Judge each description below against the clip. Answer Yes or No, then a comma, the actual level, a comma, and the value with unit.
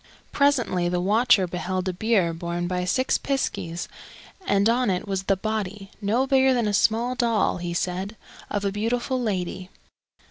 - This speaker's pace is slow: No, average, 165 wpm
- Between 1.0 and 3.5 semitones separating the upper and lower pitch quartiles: No, average, 4.4 semitones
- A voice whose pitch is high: Yes, high, 200 Hz